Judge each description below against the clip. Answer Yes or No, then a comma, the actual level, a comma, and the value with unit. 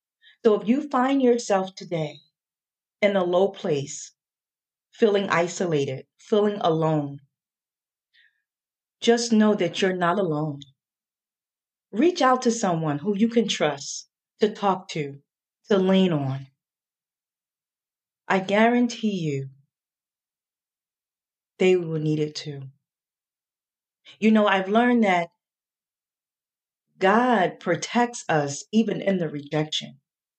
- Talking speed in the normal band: No, slow, 105 wpm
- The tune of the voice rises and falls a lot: Yes, wide, 5.9 semitones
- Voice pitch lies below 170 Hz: No, high, 190 Hz